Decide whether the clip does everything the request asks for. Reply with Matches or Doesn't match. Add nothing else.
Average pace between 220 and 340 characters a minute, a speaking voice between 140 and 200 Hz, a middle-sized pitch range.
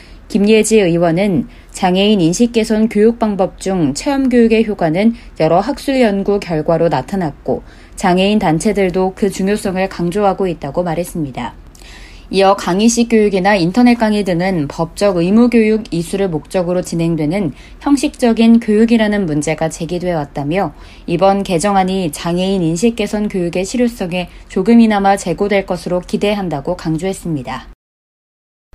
Matches